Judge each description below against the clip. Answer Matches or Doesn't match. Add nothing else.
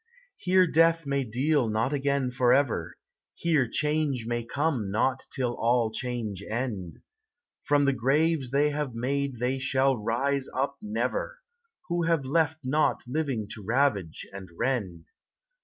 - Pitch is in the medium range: Doesn't match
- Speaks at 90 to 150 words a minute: Matches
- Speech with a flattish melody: Doesn't match